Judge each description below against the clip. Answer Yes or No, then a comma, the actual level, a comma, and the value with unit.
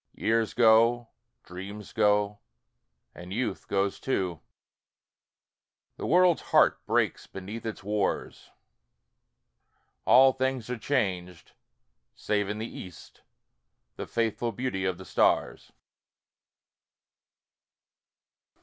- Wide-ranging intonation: No, average, 3.7 semitones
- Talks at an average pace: No, slow, 95 wpm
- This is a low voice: Yes, low, 105 Hz